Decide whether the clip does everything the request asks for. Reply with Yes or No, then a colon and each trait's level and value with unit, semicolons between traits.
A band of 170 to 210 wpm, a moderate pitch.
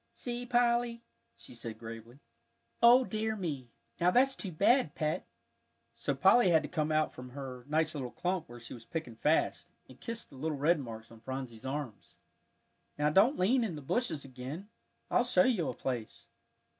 Yes: average, 180 wpm; medium, 155 Hz